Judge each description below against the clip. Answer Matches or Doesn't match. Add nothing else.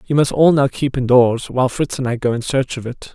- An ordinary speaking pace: Doesn't match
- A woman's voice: Doesn't match